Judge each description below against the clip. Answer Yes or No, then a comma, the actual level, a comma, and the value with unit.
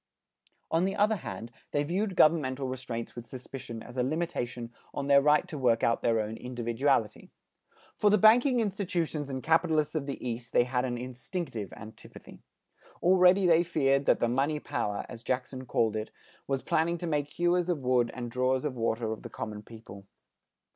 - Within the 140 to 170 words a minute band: No, average, 180 wpm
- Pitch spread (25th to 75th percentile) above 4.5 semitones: Yes, wide, 5.6 semitones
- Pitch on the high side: No, low, 130 Hz